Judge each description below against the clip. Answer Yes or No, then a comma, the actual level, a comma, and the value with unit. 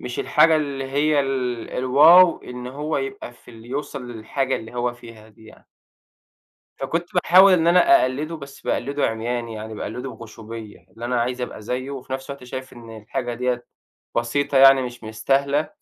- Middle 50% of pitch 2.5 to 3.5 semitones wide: Yes, average, 3.0 semitones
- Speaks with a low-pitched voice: Yes, low, 125 Hz